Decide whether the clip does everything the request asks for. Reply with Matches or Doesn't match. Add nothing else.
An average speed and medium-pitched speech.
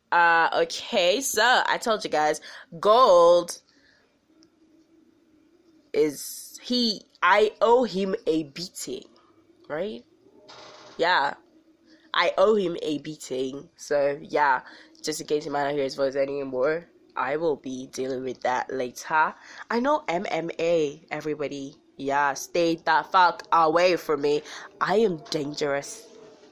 Doesn't match